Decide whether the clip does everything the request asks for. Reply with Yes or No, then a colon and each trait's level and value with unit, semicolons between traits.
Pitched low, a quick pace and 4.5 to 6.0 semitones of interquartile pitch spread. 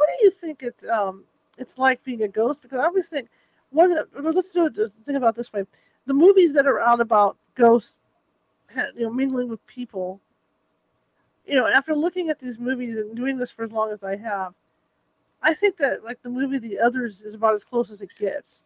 No: high, 245 Hz; fast, 220 wpm; average, 4.8 semitones